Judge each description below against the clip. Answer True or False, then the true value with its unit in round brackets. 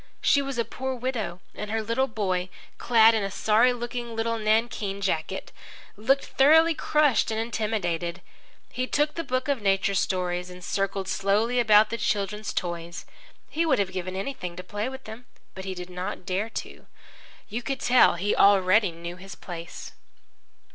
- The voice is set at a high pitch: True (210 Hz)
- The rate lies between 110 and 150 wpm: False (170 wpm)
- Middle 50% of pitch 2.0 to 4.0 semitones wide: False (4.4 semitones)